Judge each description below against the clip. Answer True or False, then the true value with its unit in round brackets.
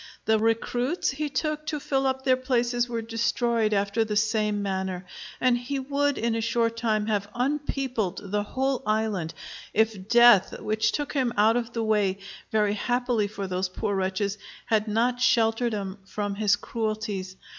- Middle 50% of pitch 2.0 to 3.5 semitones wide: True (3.0 semitones)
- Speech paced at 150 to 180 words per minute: True (165 wpm)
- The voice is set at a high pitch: True (225 Hz)